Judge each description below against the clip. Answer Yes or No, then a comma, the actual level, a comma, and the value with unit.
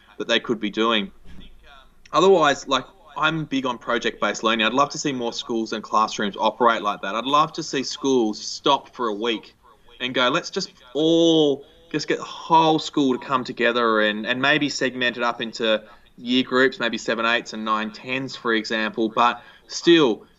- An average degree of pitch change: Yes, average, 3.7 semitones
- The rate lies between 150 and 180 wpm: No, average, 190 wpm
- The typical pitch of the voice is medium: No, low, 125 Hz